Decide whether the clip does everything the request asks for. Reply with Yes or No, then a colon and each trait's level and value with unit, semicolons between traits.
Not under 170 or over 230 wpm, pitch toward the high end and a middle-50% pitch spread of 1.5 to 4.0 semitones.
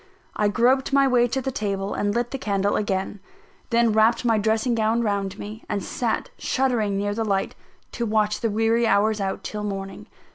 Yes: average, 190 wpm; high, 220 Hz; narrow, 2.5 semitones